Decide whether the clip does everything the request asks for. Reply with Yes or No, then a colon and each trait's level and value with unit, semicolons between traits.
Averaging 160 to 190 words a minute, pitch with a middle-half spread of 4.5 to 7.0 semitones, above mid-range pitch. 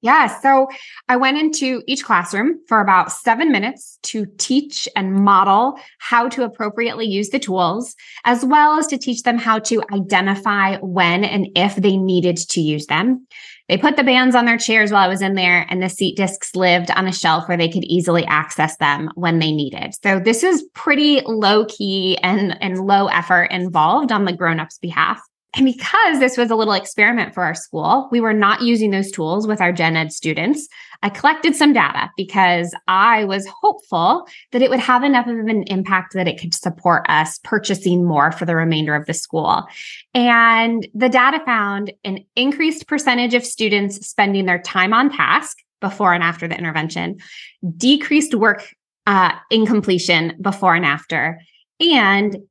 Yes: average, 180 wpm; average, 5.2 semitones; high, 200 Hz